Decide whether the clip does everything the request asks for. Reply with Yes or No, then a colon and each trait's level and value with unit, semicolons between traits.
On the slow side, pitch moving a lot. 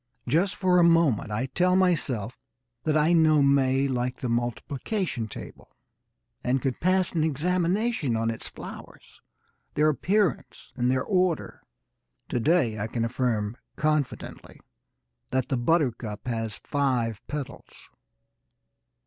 Yes: slow, 125 wpm; wide, 5.7 semitones